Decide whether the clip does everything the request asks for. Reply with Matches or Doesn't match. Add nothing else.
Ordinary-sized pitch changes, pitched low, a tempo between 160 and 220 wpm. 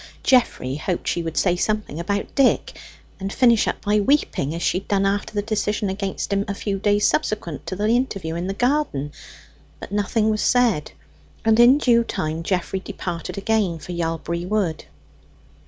Doesn't match